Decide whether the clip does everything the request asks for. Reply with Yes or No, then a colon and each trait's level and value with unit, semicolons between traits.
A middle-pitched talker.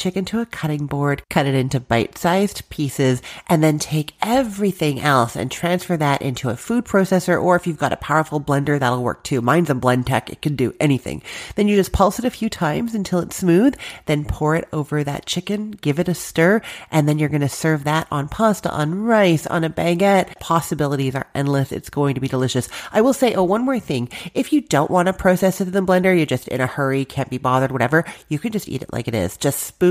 Yes: medium, 155 Hz